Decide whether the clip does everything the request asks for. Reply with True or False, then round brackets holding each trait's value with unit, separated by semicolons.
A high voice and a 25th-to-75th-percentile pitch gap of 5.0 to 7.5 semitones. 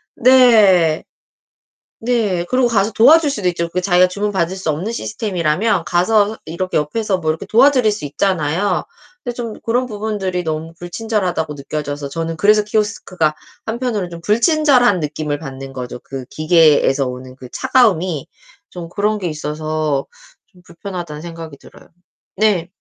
False (180 Hz; 5.5 semitones)